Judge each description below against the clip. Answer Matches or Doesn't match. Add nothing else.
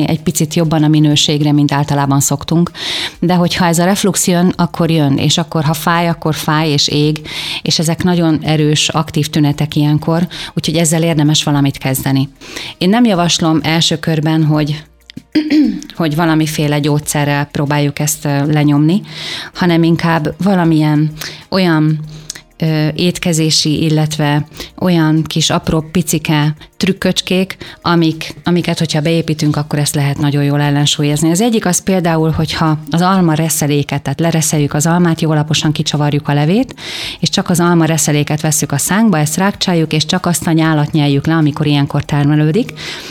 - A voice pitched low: Doesn't match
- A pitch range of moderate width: Doesn't match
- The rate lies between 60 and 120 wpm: Doesn't match